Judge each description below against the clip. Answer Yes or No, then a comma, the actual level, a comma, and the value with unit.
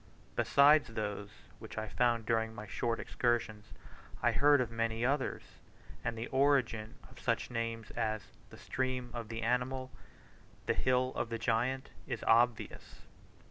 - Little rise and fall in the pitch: Yes, narrow, 2.3 semitones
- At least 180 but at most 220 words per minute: No, average, 145 wpm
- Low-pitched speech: Yes, low, 115 Hz